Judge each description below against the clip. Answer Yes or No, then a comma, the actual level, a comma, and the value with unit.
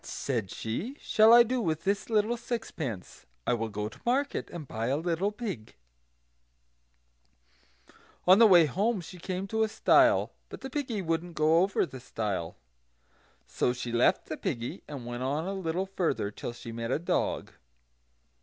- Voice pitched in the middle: Yes, medium, 165 Hz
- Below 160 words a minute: No, average, 175 wpm